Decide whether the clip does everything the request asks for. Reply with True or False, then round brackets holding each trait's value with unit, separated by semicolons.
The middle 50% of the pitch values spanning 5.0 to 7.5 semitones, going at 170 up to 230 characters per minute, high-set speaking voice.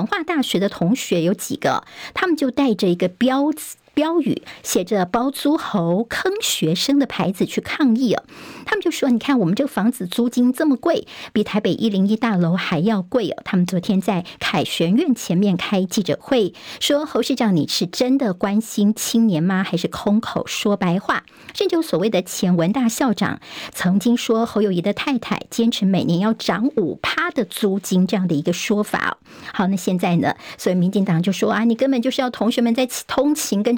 False (5.4 semitones; 290 characters per minute; 220 Hz)